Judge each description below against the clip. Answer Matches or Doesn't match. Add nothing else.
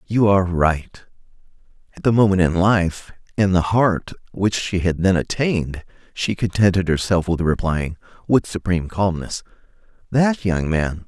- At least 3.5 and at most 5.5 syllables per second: Matches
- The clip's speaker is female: Doesn't match